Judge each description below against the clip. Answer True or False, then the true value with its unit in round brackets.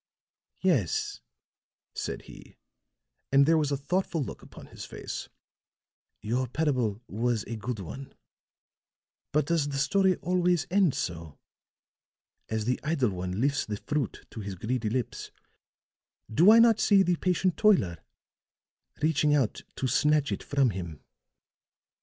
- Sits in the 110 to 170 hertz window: True (140 Hz)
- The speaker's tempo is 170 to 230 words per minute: False (135 wpm)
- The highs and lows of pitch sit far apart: True (7.2 semitones)